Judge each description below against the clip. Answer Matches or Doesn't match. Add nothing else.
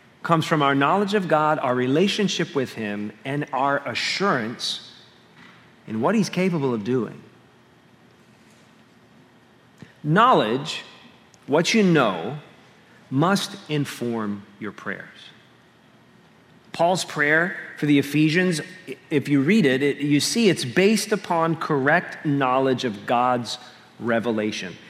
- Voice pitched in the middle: Matches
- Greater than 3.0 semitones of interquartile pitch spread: Matches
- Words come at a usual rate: Doesn't match